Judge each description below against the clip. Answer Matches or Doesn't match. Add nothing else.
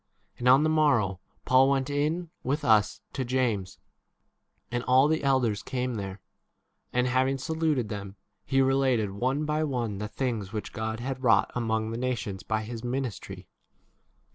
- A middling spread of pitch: Matches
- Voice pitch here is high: Doesn't match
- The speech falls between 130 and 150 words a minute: Doesn't match